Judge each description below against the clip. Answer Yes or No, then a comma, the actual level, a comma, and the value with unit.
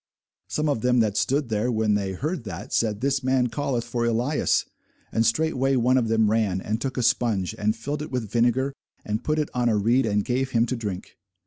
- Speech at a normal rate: No, fast, 220 wpm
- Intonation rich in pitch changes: No, average, 3.3 semitones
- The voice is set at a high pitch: No, low, 120 Hz